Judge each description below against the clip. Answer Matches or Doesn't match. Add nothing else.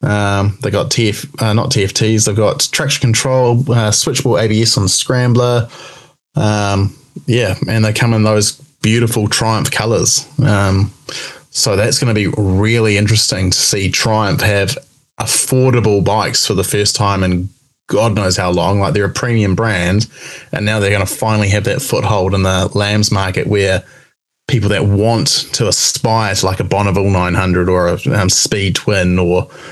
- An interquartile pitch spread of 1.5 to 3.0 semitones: Doesn't match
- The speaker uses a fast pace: Doesn't match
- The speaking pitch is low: Matches